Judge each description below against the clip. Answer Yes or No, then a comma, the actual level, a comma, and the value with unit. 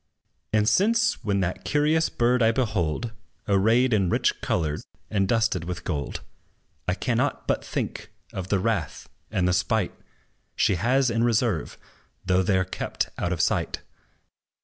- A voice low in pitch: Yes, low, 105 Hz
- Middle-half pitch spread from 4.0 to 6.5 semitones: Yes, average, 4.8 semitones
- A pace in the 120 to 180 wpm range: Yes, average, 150 wpm